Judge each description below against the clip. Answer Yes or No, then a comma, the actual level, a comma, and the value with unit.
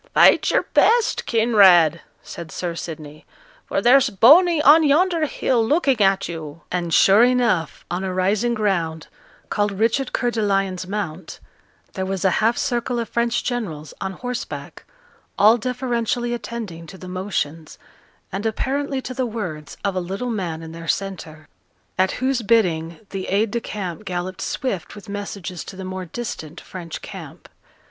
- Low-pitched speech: No, high, 200 Hz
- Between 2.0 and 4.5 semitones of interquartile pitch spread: No, average, 5.2 semitones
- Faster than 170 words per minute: No, average, 160 wpm